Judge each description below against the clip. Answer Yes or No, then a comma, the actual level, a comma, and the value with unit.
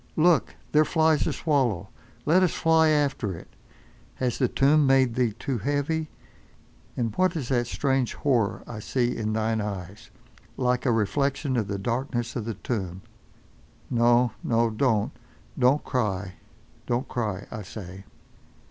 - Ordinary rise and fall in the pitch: Yes, average, 4.4 semitones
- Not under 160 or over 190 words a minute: No, average, 140 wpm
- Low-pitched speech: Yes, low, 120 Hz